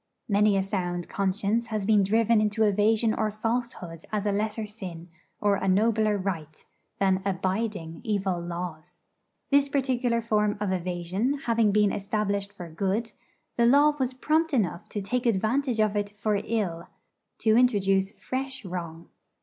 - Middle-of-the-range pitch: No, high, 210 Hz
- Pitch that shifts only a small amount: No, average, 3.2 semitones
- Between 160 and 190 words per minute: No, average, 150 wpm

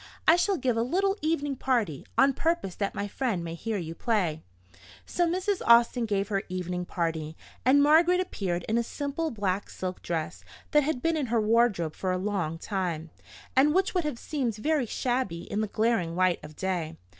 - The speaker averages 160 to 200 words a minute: Yes, average, 190 wpm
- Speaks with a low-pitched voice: No, high, 225 Hz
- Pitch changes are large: Yes, wide, 7.9 semitones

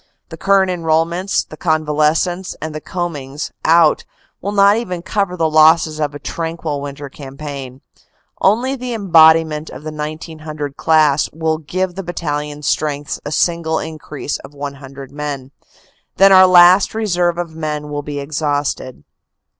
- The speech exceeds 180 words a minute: No, average, 145 wpm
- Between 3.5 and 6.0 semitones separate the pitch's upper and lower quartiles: No, average, 3.0 semitones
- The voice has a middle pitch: Yes, medium, 155 Hz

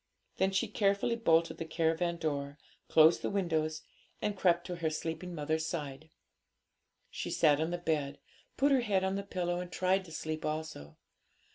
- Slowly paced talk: No, average, 170 wpm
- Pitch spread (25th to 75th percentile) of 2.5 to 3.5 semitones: Yes, average, 3.1 semitones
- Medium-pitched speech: Yes, medium, 165 Hz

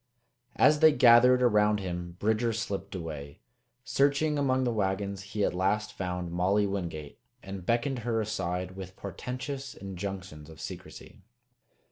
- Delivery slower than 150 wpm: Yes, slow, 135 wpm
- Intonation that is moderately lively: Yes, average, 4.7 semitones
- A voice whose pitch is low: Yes, low, 100 Hz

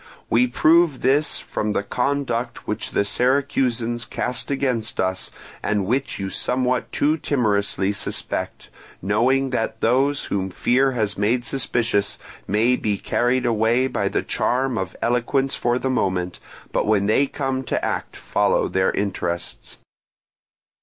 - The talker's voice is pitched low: Yes, low, 120 Hz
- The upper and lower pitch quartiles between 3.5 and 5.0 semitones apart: Yes, average, 4.3 semitones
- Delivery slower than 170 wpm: Yes, average, 140 wpm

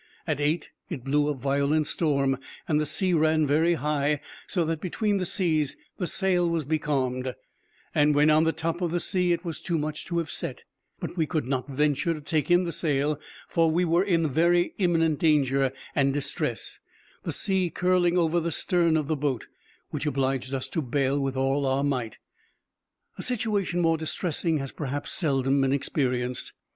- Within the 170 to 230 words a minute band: Yes, average, 185 wpm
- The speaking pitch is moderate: Yes, medium, 155 Hz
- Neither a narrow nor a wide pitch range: Yes, average, 3.5 semitones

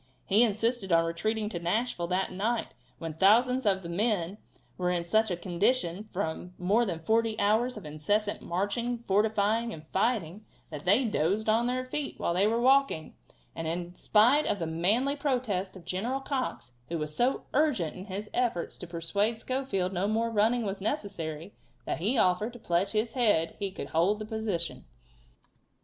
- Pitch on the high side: Yes, high, 205 Hz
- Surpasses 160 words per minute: Yes, average, 175 wpm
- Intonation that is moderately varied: Yes, average, 4.8 semitones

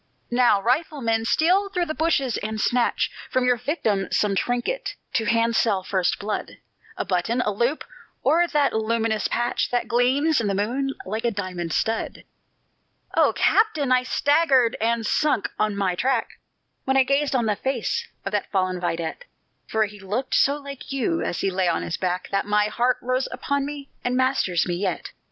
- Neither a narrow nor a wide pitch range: Yes, average, 4.9 semitones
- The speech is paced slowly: No, average, 180 wpm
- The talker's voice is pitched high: Yes, high, 235 Hz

